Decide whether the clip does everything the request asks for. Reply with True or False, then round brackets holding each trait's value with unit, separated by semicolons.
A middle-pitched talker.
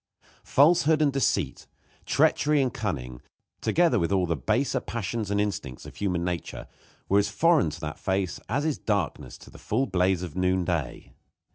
False (100 Hz)